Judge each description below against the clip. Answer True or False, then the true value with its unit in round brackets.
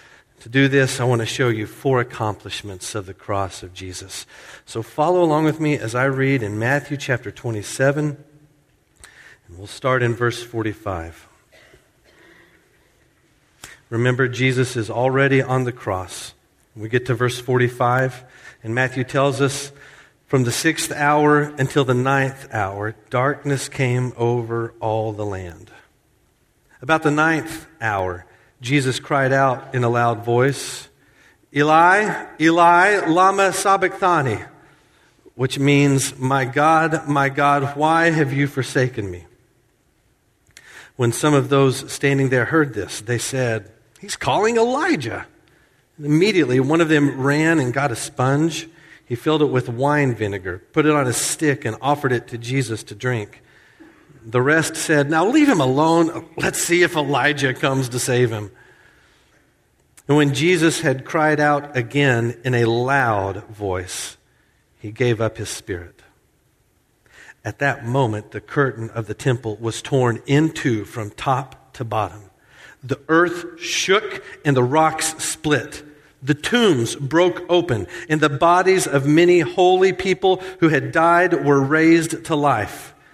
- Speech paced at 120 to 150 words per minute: True (145 wpm)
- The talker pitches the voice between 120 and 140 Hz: True (135 Hz)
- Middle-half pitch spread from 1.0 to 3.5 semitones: False (4.5 semitones)